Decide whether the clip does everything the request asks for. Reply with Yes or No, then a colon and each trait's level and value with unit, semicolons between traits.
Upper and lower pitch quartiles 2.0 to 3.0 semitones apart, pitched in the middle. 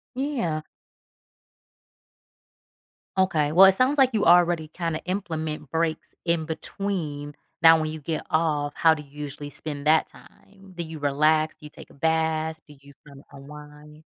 Yes: narrow, 2.4 semitones; medium, 160 Hz